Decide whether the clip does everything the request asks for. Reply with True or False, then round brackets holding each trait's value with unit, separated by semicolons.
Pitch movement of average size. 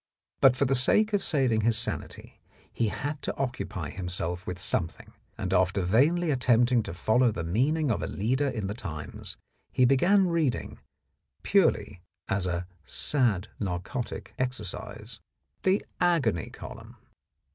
False (6.3 semitones)